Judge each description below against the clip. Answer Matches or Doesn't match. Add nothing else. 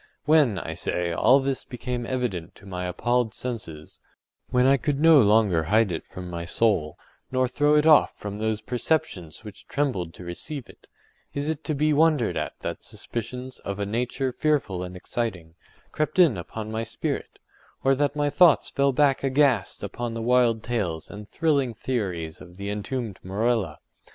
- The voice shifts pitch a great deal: Matches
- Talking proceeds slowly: Doesn't match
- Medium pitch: Doesn't match